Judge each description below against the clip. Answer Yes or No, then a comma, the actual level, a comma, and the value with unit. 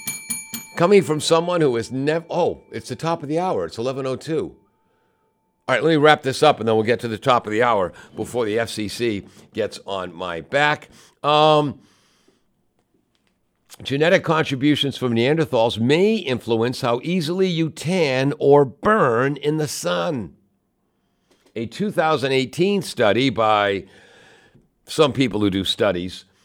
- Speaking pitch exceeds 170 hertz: No, low, 135 Hz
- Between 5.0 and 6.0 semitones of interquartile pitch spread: Yes, wide, 5.4 semitones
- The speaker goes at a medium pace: Yes, average, 145 wpm